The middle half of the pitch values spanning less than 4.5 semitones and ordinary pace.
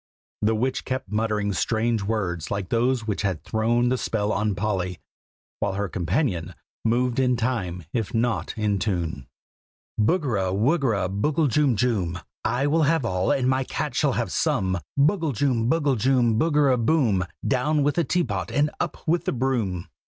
No: average, 4.9 semitones; average, 165 wpm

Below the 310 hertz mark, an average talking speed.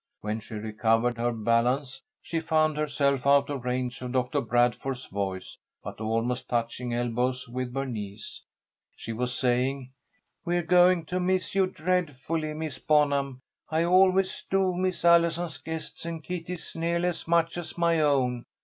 Yes: medium, 140 Hz; average, 150 wpm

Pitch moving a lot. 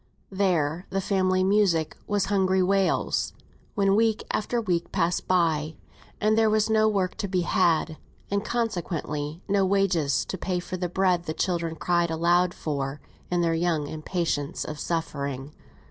No: average, 3.3 semitones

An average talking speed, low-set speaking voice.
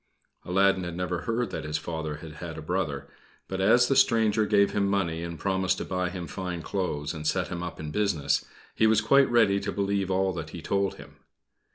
No: fast, 215 wpm; very low, 95 Hz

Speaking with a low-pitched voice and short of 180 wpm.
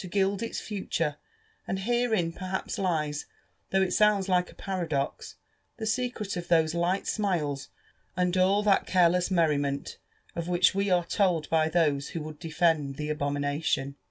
No: medium, 175 Hz; average, 155 wpm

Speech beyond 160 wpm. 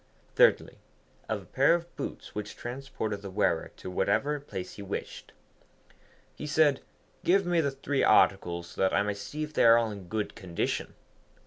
Yes: average, 180 wpm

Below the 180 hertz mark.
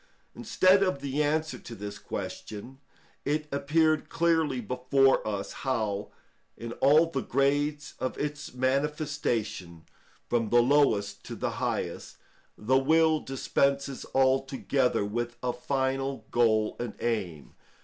Yes: low, 135 Hz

